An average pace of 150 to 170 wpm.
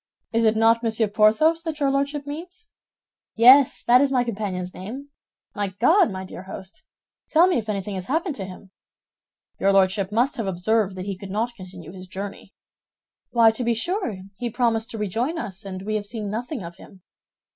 No: average, 190 wpm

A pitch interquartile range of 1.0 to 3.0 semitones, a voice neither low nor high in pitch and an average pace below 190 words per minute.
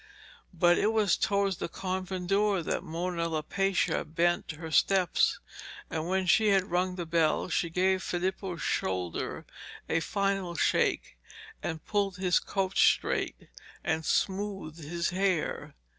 Yes: average, 2.7 semitones; medium, 180 Hz; slow, 135 wpm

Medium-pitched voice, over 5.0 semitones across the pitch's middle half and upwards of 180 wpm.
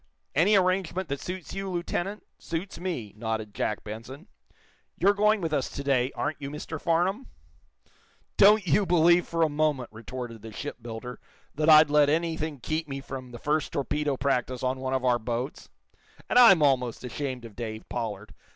No: medium, 145 Hz; wide, 5.6 semitones; average, 170 wpm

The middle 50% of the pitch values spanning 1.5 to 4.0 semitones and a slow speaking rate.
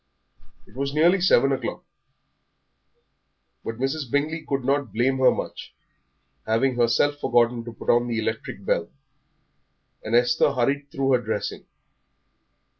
Yes: average, 3.0 semitones; slow, 130 wpm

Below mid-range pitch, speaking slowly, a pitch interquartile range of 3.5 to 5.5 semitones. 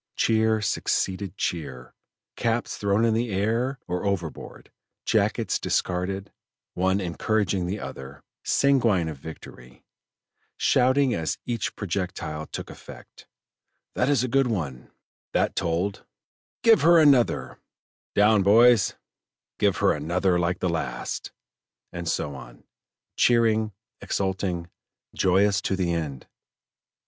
Yes: very low, 95 Hz; slow, 115 wpm; average, 4.9 semitones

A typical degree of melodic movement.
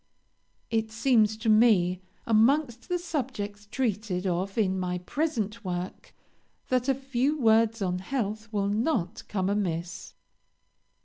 Yes: average, 4.3 semitones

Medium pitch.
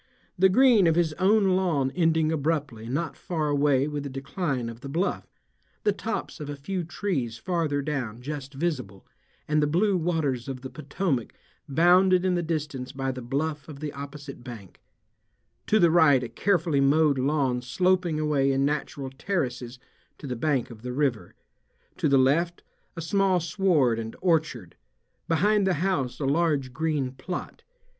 Yes: medium, 150 Hz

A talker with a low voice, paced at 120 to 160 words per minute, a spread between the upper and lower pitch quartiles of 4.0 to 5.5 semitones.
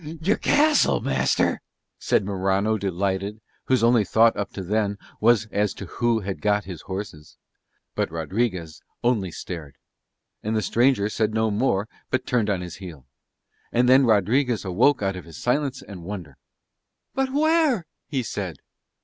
Yes: low, 105 Hz; average, 155 wpm; average, 4.5 semitones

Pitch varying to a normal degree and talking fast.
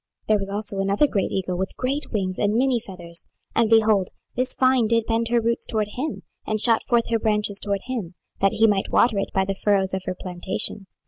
Yes: average, 3.1 semitones; fast, 220 wpm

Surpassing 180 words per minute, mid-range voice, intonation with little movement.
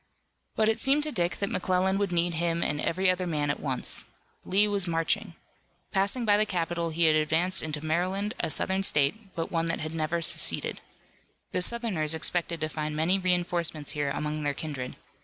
No: average, 190 wpm; medium, 170 Hz; average, 3.6 semitones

